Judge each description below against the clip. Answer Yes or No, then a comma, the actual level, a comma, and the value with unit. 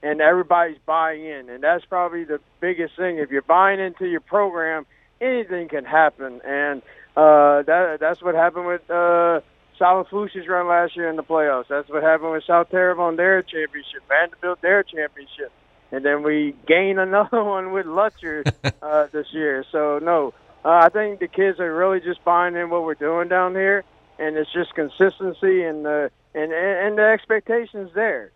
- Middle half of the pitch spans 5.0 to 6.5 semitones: No, average, 3.4 semitones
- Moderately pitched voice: Yes, medium, 170 Hz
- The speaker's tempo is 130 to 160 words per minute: No, average, 175 wpm